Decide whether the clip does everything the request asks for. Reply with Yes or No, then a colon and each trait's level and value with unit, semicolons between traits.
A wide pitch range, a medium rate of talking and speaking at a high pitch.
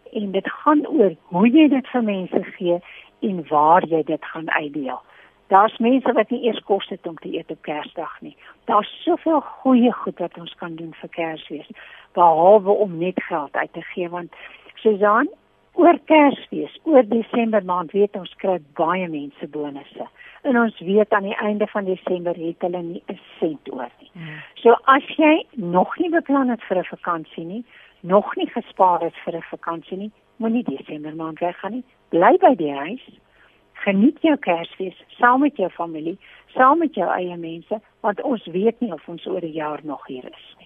Yes: wide, 5.9 semitones; average, 185 wpm; high, 200 Hz